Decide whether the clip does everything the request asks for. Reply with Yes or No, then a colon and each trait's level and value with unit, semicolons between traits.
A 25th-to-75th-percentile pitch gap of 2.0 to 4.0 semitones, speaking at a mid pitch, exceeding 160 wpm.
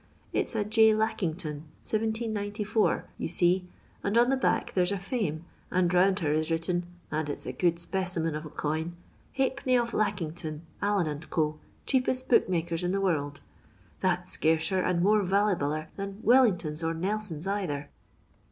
No: average, 4.5 semitones; medium, 180 Hz; average, 170 wpm